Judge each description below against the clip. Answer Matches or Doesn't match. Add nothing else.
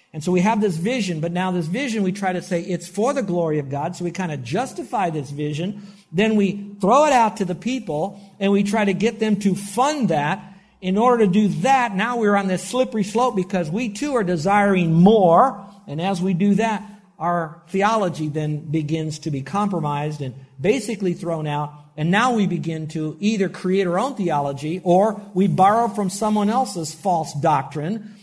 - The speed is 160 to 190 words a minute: Doesn't match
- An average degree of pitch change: Matches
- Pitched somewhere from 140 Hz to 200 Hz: Matches